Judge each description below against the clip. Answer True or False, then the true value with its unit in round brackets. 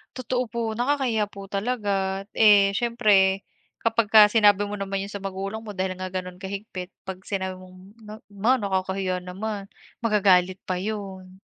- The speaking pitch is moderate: False (200 Hz)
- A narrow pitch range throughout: True (2.3 semitones)